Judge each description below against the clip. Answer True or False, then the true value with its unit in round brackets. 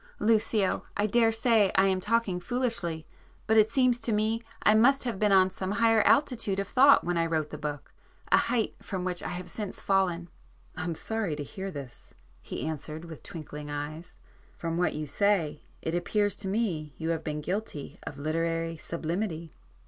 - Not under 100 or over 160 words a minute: False (170 wpm)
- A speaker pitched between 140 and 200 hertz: True (185 Hz)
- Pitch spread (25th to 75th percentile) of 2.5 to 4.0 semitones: False (5.3 semitones)